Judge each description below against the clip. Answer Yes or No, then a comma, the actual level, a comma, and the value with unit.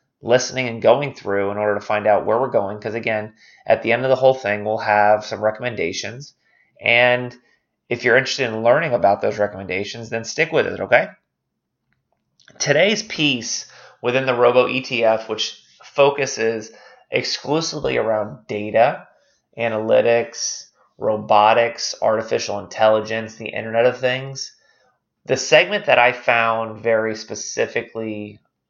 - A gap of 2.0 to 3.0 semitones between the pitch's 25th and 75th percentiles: Yes, average, 2.7 semitones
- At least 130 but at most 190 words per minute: Yes, slow, 135 wpm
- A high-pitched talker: No, low, 115 Hz